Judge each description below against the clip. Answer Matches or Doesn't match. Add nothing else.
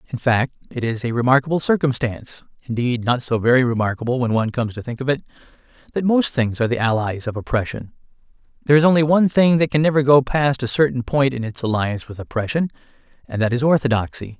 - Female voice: Doesn't match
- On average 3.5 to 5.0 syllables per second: Doesn't match